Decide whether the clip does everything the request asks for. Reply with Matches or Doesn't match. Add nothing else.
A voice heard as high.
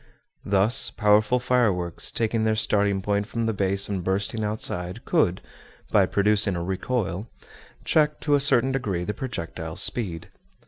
Doesn't match